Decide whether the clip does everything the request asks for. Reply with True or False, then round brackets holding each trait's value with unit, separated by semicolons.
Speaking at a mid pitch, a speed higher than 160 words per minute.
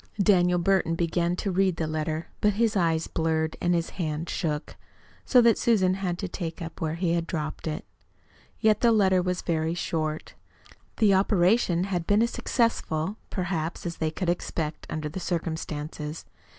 True (175 Hz; 175 wpm)